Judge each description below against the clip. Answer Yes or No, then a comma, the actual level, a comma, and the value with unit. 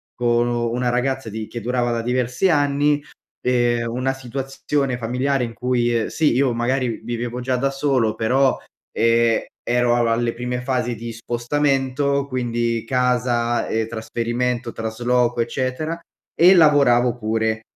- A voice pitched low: Yes, low, 120 Hz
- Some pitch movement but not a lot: No, narrow, 2.1 semitones